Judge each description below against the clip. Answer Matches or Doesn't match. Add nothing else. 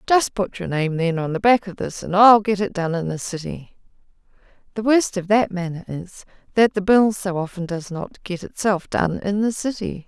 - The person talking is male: Doesn't match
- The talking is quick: Matches